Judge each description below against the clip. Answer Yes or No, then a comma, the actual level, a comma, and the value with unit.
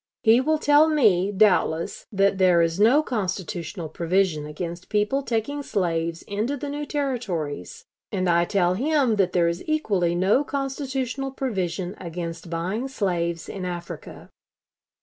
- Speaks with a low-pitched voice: No, high, 195 Hz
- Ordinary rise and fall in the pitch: No, wide, 7.4 semitones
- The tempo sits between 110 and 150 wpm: Yes, average, 140 wpm